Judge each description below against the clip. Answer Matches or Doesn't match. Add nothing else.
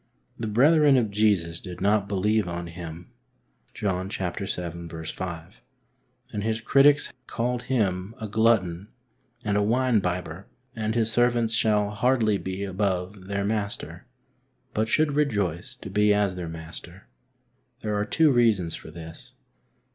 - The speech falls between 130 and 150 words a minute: Matches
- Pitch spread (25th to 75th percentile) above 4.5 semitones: Doesn't match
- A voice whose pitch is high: Doesn't match